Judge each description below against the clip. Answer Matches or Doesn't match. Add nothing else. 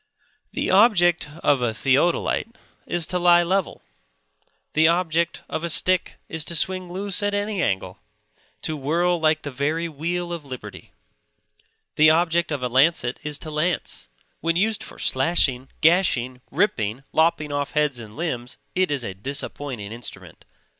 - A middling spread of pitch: Matches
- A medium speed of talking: Matches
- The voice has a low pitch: Doesn't match